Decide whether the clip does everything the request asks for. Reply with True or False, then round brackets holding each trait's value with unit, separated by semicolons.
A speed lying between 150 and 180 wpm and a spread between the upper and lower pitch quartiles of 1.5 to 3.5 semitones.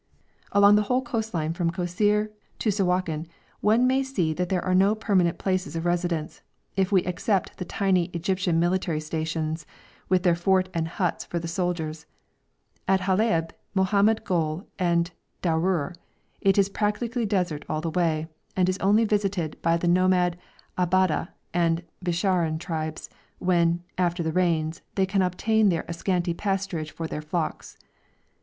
True (155 wpm; 2.6 semitones)